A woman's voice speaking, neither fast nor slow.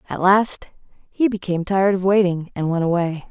Yes: female; average, 180 wpm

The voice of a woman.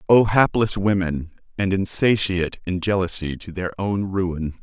No: male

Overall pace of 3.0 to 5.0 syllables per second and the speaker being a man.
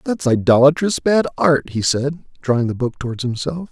No: 5.2 syllables/s; male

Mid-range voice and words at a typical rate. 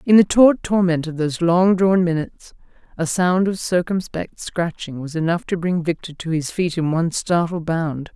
Yes: medium, 170 Hz; average, 190 wpm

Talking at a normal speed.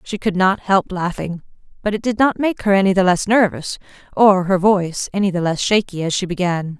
No: fast, 220 wpm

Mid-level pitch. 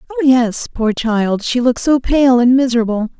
No: high, 240 Hz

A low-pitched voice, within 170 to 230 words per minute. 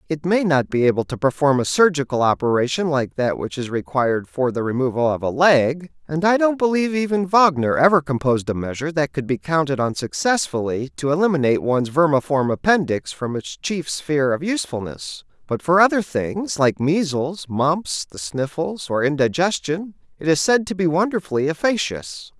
No: medium, 150 Hz; average, 175 wpm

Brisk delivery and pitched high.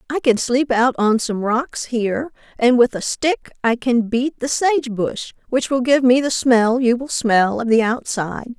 Yes: fast, 210 wpm; high, 245 Hz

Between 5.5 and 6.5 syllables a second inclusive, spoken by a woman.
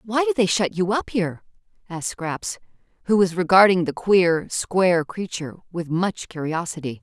No: 4.9 syllables/s; female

